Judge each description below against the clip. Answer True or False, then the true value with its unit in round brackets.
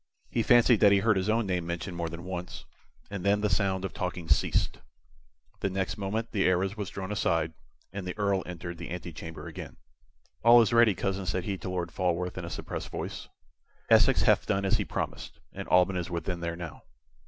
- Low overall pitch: True (95 Hz)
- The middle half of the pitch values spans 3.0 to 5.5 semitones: False (2.5 semitones)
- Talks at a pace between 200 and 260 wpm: True (205 wpm)